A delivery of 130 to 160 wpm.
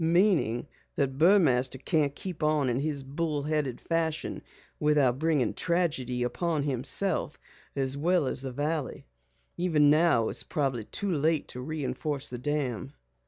Yes: average, 140 wpm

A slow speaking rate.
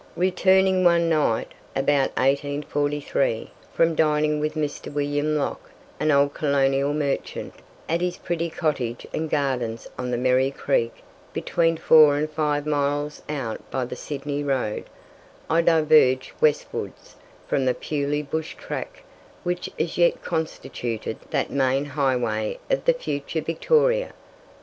Yes: slow, 130 wpm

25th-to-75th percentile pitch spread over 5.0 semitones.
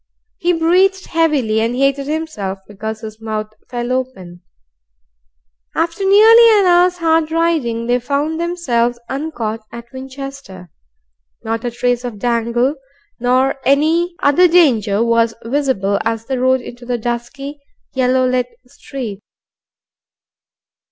Yes: wide, 5.5 semitones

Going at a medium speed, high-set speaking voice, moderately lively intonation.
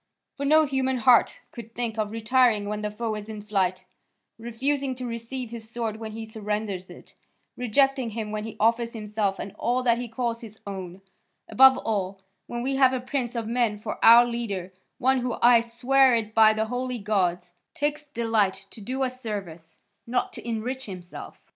Yes: average, 185 wpm; high, 230 Hz; average, 3.0 semitones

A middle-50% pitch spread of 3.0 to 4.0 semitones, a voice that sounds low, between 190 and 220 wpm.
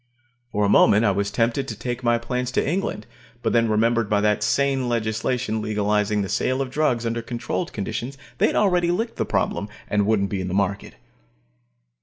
Yes: average, 3.3 semitones; low, 115 Hz; average, 195 wpm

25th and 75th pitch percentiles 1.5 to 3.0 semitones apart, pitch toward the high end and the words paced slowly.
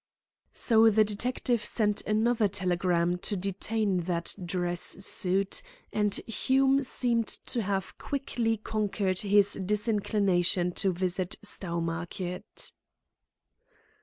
No: average, 3.4 semitones; high, 200 Hz; slow, 100 wpm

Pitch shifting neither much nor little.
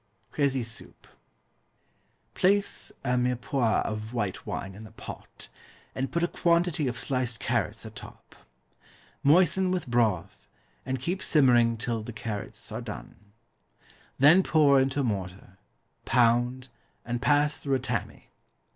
Yes: average, 4.2 semitones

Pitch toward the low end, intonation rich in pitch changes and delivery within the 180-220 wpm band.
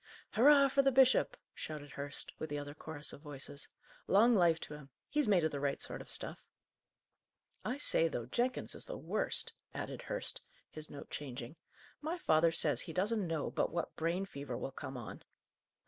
No: medium, 160 Hz; wide, 8.0 semitones; average, 185 wpm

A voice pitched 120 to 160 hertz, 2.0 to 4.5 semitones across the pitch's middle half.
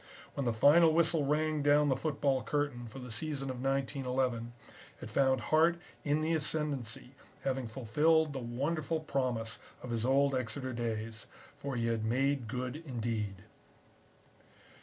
Yes: low, 135 Hz; average, 3.9 semitones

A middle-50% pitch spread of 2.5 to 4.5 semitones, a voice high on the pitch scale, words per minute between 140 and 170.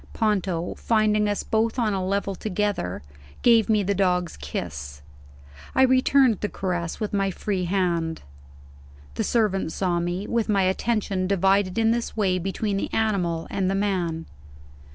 Yes: average, 3.1 semitones; high, 195 Hz; average, 155 wpm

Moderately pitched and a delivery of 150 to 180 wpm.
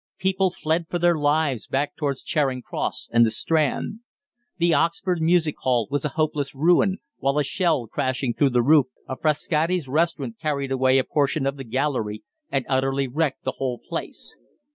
Yes: medium, 145 Hz; average, 175 wpm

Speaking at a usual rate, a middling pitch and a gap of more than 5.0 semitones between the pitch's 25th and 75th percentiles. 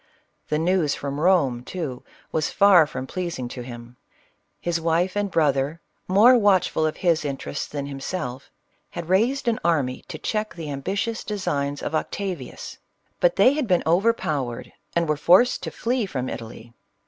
Yes: average, 160 wpm; medium, 165 Hz; wide, 5.5 semitones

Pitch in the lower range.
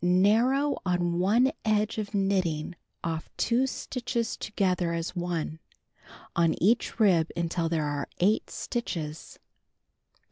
No: medium, 180 Hz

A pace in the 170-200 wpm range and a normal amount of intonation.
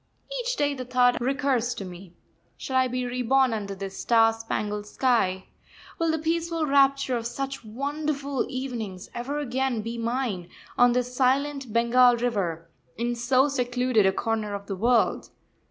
No: average, 155 wpm; average, 3.2 semitones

